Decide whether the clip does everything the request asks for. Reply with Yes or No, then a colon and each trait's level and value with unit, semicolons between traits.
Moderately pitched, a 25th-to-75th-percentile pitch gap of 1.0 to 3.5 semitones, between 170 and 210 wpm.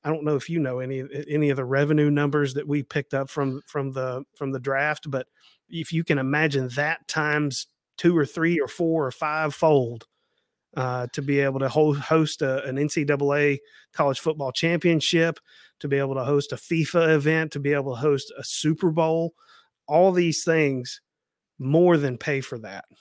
Yes: medium, 145 Hz; average, 2.7 semitones; average, 190 wpm